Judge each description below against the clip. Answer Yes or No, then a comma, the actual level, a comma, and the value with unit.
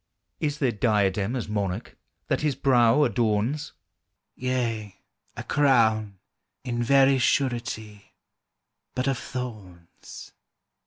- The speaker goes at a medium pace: No, slow, 100 wpm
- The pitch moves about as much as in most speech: Yes, average, 3.9 semitones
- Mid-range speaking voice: No, low, 120 Hz